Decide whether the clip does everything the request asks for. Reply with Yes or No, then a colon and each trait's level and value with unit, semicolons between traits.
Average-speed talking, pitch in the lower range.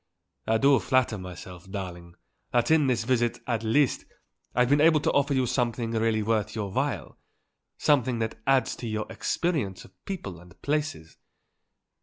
Yes: average, 160 wpm; low, 115 Hz